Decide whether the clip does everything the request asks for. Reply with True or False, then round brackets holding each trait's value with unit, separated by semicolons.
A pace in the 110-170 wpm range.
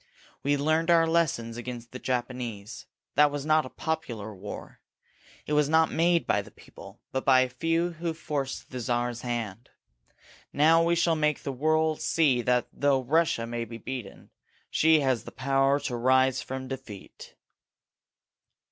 True (160 wpm)